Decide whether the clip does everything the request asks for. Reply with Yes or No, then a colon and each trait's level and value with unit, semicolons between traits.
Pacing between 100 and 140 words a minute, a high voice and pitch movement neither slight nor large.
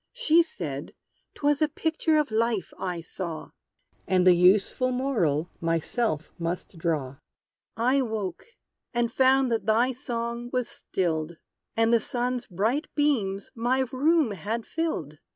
No: slow, 135 wpm; high, 230 Hz; wide, 6.4 semitones